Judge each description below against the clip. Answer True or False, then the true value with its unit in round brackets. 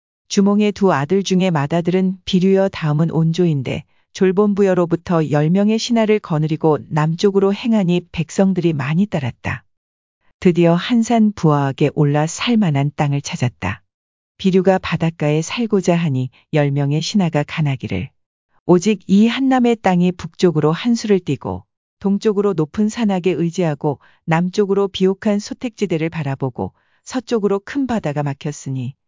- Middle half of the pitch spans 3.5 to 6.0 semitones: True (5.3 semitones)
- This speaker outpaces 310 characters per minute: True (320 characters per minute)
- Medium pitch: True (175 Hz)